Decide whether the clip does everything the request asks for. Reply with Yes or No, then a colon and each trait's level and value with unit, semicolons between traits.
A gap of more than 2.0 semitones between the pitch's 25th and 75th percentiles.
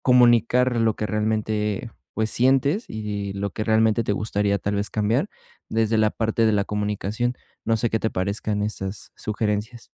No: narrow, 1.7 semitones